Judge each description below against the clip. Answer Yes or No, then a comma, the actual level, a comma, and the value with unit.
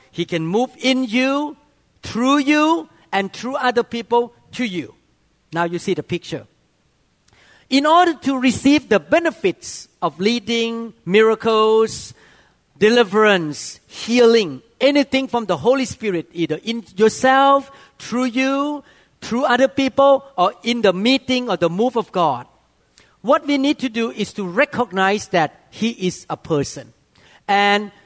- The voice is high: Yes, high, 235 Hz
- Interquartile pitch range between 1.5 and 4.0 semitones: No, average, 5.3 semitones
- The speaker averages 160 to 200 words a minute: No, average, 140 wpm